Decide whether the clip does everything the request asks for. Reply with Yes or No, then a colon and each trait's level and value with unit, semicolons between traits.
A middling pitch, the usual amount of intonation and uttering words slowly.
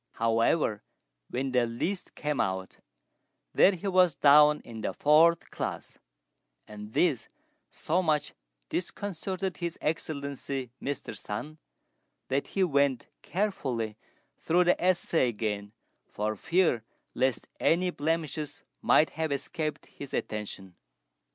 No: medium, 145 Hz; wide, 6.4 semitones; slow, 115 wpm